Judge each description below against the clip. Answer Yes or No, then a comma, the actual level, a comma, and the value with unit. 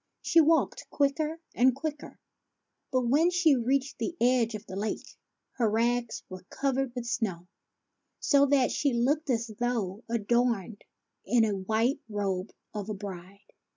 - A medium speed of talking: Yes, average, 150 wpm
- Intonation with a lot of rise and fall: No, average, 4.6 semitones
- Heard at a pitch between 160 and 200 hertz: No, high, 240 Hz